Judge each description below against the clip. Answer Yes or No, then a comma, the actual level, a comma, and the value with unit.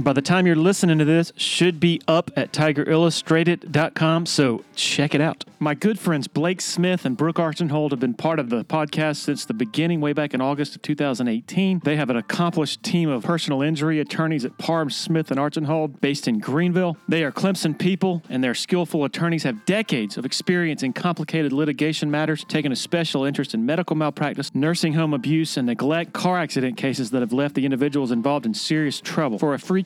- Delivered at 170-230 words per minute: Yes, average, 200 wpm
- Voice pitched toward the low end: No, medium, 155 Hz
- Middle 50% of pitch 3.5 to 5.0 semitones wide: No, average, 2.9 semitones